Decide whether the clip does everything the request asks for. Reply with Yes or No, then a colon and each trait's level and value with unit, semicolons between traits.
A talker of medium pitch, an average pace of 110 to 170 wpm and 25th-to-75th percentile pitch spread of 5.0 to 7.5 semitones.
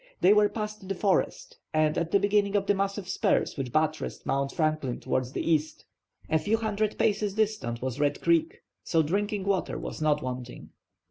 No: medium, 180 Hz; average, 185 wpm; average, 5.3 semitones